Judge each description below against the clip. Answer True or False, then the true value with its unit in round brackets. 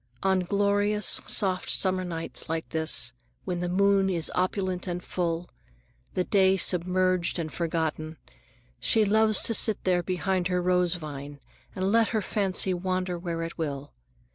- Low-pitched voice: False (180 Hz)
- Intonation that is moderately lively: False (2.3 semitones)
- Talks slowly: False (150 wpm)